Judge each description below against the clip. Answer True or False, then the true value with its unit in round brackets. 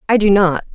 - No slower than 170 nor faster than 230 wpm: False (245 wpm)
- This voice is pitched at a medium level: False (195 Hz)